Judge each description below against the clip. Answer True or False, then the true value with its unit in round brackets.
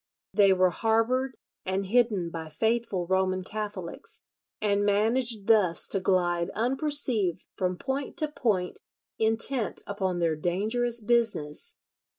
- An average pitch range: True (4.2 semitones)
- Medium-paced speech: False (120 wpm)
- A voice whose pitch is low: False (205 Hz)